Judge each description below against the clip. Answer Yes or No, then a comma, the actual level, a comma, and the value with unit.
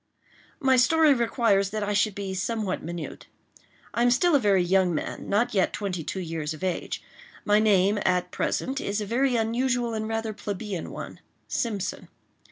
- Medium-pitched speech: No, high, 210 Hz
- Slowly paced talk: No, average, 165 wpm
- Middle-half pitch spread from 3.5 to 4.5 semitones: Yes, average, 3.9 semitones